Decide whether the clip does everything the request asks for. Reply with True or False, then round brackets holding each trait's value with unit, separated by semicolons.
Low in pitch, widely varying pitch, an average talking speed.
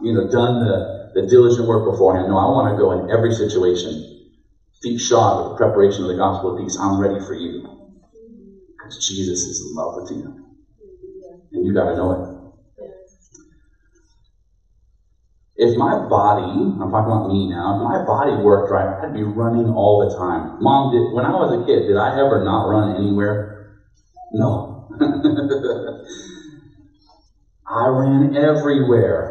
True (110 Hz; 7.0 semitones; 160 wpm)